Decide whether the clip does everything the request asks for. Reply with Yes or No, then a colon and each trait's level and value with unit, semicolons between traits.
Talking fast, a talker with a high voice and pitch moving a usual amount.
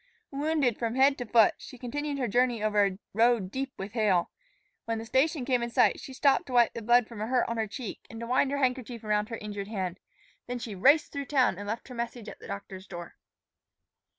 Yes: fast, 235 wpm; high, 235 Hz; average, 3.6 semitones